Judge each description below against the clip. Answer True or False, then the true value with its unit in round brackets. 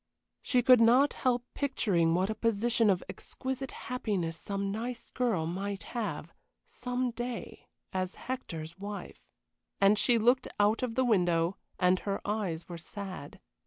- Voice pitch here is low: False (210 Hz)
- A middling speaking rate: True (145 wpm)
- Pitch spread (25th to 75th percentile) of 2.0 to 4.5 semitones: False (4.9 semitones)